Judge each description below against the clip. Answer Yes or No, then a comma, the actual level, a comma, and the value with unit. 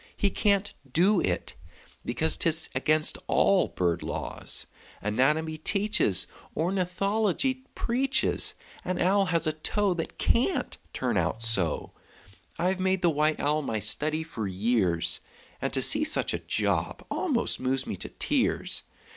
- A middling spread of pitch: No, wide, 7.8 semitones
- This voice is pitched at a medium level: Yes, medium, 160 Hz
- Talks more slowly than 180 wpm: Yes, average, 140 wpm